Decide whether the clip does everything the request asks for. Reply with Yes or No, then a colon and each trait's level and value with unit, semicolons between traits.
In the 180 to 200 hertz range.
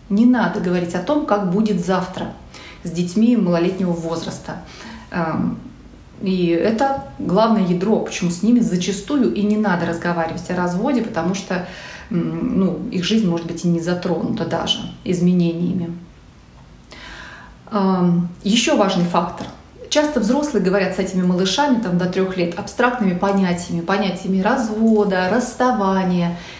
Yes: high, 190 Hz